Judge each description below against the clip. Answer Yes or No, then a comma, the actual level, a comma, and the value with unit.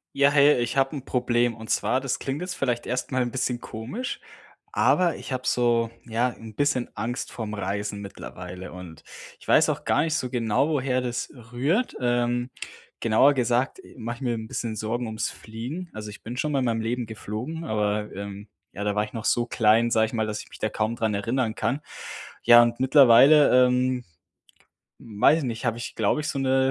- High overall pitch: No, low, 120 Hz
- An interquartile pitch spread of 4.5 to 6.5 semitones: No, average, 3.1 semitones